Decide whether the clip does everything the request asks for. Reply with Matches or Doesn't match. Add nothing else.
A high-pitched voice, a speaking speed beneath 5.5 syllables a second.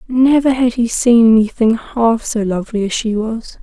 Matches